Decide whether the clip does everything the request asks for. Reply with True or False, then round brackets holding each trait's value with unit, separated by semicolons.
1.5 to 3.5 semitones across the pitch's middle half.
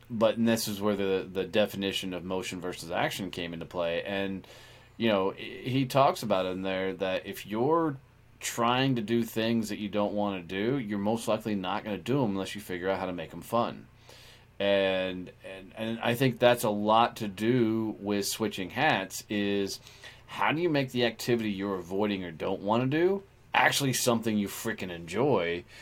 False (3.9 semitones)